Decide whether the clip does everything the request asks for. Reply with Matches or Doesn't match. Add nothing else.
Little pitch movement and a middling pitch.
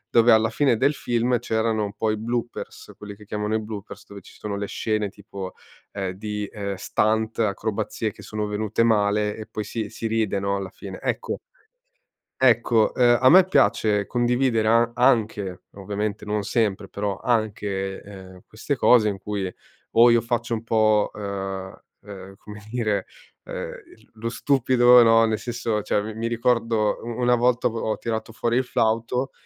Doesn't match